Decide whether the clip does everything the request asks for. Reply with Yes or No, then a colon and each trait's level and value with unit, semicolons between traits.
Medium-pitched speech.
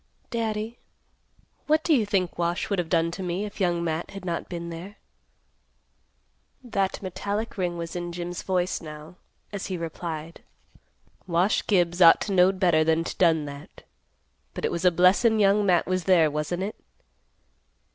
Yes: medium, 180 Hz